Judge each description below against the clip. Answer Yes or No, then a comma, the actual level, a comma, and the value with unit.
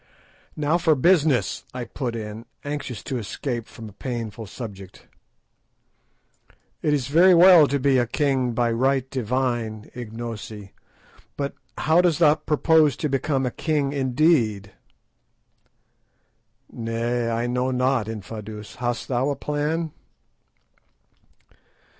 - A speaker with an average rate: No, slow, 120 wpm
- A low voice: Yes, low, 125 Hz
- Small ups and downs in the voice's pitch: No, average, 4.2 semitones